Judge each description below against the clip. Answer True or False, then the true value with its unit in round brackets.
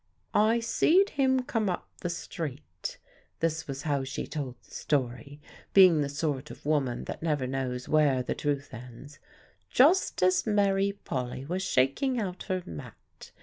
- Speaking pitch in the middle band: True (155 Hz)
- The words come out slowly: False (155 wpm)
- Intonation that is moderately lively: False (6.8 semitones)